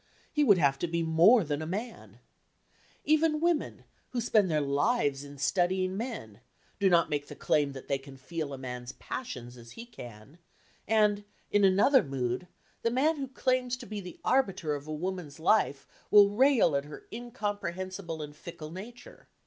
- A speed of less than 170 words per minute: No, average, 175 wpm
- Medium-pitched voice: Yes, medium, 180 Hz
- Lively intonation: Yes, wide, 8.1 semitones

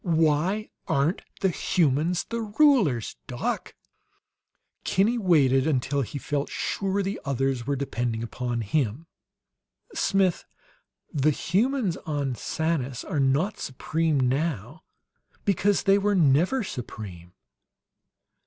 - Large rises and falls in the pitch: Yes, wide, 6.5 semitones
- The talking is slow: Yes, slow, 105 wpm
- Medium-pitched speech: Yes, medium, 150 Hz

